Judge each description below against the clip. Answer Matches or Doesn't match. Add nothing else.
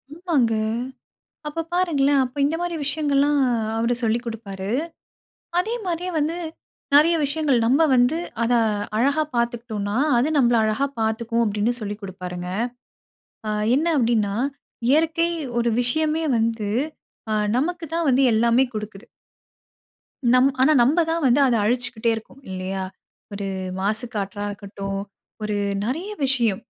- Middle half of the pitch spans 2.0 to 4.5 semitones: Doesn't match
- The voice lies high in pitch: Matches